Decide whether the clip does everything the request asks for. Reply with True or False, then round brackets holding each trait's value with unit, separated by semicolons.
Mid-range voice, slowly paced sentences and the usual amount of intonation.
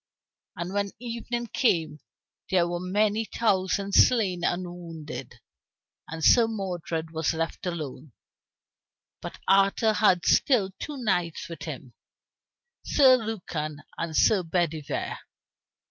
True (180 Hz; 115 wpm; 4.7 semitones)